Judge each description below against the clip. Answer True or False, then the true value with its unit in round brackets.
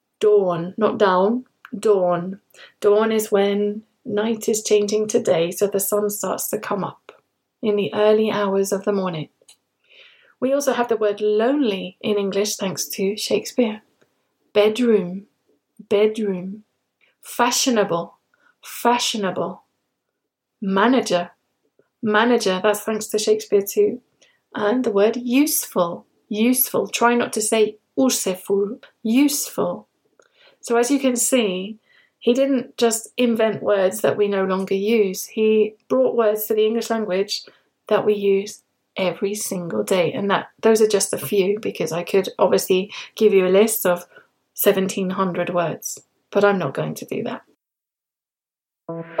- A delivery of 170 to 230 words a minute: False (135 wpm)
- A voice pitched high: True (210 Hz)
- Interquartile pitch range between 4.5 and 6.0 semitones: False (2.9 semitones)